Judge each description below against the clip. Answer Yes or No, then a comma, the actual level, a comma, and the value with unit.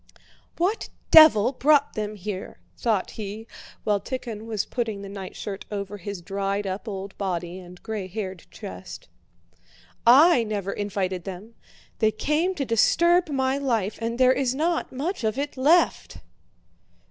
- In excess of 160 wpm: No, average, 140 wpm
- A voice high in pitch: Yes, high, 215 Hz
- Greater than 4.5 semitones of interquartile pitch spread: Yes, average, 5.1 semitones